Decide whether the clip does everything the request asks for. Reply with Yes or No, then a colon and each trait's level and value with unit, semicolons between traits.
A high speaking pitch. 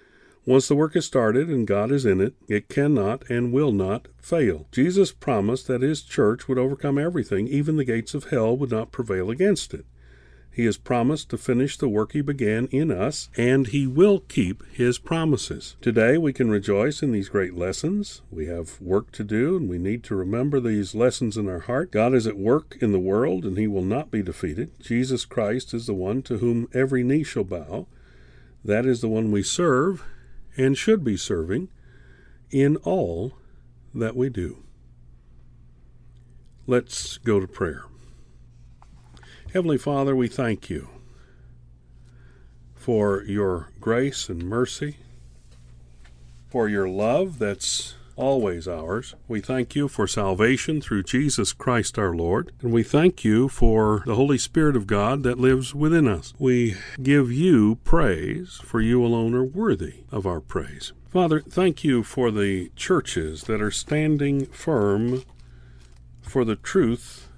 No: low, 115 Hz